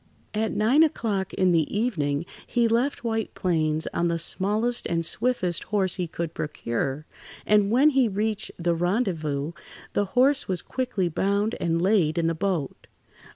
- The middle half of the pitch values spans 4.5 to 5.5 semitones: Yes, average, 5.0 semitones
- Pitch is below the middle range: No, high, 190 Hz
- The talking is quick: No, average, 155 wpm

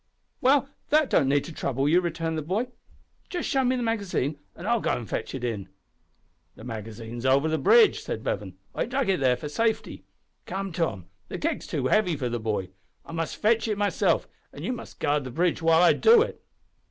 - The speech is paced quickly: Yes, fast, 210 wpm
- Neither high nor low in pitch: Yes, medium, 165 Hz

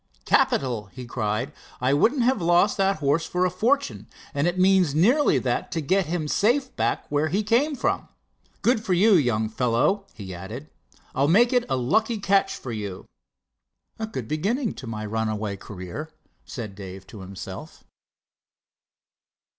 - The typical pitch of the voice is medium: Yes, medium, 155 Hz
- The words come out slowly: No, average, 160 wpm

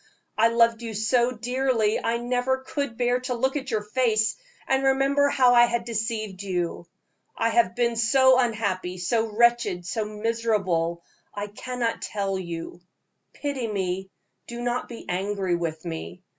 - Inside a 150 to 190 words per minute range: Yes, average, 155 wpm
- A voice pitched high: Yes, high, 230 Hz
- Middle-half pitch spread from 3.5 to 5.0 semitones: Yes, average, 3.8 semitones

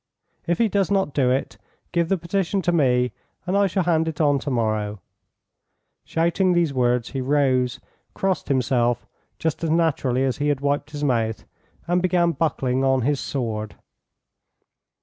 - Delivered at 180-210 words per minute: No, average, 165 wpm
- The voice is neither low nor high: Yes, medium, 145 Hz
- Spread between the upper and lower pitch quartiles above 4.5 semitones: Yes, average, 5.2 semitones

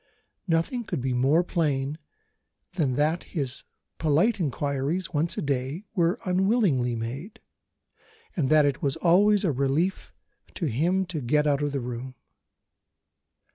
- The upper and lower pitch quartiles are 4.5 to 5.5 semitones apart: Yes, average, 4.8 semitones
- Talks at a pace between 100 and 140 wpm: Yes, slow, 135 wpm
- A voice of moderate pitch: Yes, medium, 150 Hz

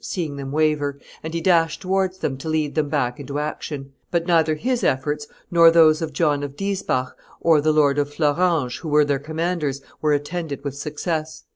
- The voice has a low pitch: No, medium, 155 Hz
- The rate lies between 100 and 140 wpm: No, average, 190 wpm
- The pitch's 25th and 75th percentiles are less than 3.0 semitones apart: Yes, narrow, 2.5 semitones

